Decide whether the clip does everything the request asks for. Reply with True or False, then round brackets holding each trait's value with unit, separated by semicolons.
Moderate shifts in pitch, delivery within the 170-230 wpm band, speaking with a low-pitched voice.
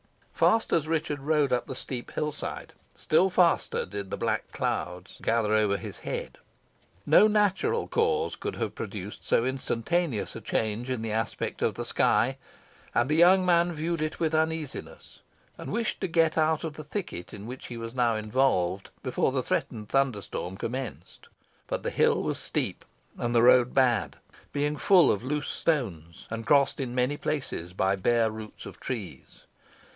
False (6.2 semitones; 175 wpm; 130 Hz)